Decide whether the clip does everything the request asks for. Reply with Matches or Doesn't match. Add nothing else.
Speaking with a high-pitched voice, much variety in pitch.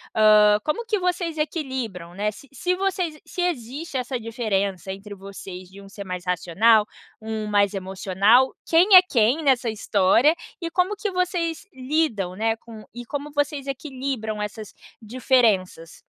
Matches